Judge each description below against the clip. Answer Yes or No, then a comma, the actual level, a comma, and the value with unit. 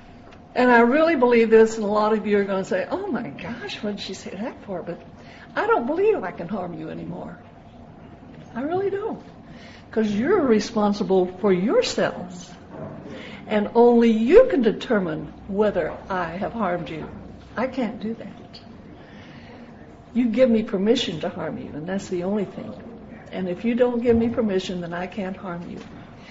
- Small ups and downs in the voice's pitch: No, average, 3.6 semitones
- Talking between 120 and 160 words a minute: No, average, 180 wpm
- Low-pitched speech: No, high, 220 Hz